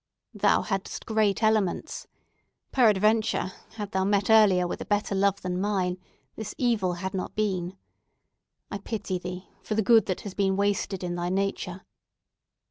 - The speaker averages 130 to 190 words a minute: Yes, average, 155 wpm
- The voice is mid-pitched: No, high, 195 Hz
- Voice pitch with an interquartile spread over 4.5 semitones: No, narrow, 2.4 semitones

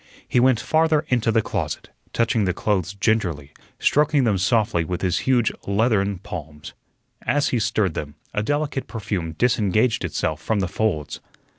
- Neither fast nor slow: Yes, average, 155 wpm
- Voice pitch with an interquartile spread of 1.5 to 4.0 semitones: No, average, 4.9 semitones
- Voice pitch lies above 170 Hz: No, low, 105 Hz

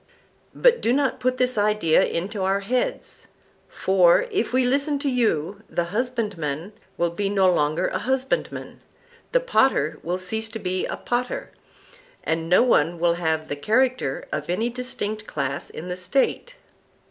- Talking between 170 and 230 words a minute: No, average, 160 wpm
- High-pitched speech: Yes, high, 205 Hz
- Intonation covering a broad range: Yes, wide, 6.6 semitones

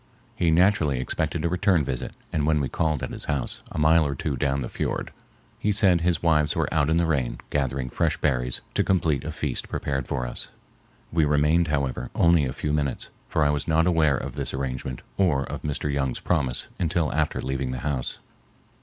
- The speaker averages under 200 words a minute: No, fast, 205 wpm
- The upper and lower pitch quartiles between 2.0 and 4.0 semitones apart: Yes, average, 3.3 semitones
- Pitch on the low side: Yes, very low, 75 Hz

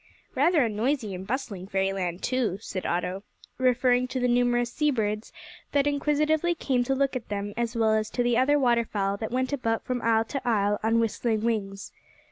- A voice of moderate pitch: No, high, 235 Hz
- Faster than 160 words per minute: Yes, average, 190 wpm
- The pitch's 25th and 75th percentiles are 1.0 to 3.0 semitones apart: No, average, 3.6 semitones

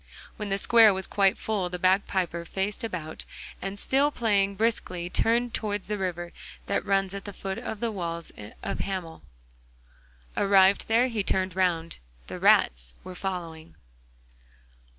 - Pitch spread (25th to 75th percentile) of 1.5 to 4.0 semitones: Yes, average, 2.8 semitones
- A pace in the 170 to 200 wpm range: No, average, 150 wpm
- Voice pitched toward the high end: Yes, high, 195 Hz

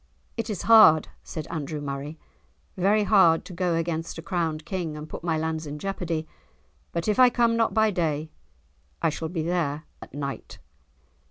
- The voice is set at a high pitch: No, medium, 165 Hz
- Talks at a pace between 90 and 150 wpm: No, average, 175 wpm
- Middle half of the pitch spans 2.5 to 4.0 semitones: Yes, average, 3.7 semitones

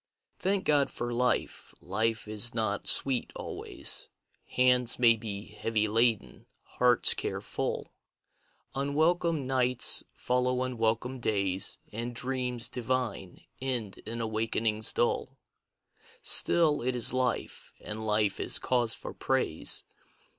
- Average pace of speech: No, slow, 115 wpm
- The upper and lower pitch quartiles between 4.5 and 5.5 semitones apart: No, narrow, 2.6 semitones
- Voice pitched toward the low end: Yes, low, 120 Hz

